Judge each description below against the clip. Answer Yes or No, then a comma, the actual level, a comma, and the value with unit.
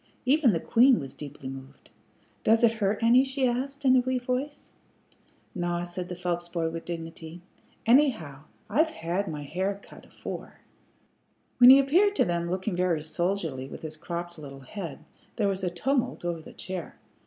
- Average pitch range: No, wide, 7.1 semitones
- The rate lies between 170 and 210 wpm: Yes, average, 175 wpm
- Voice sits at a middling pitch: Yes, medium, 180 Hz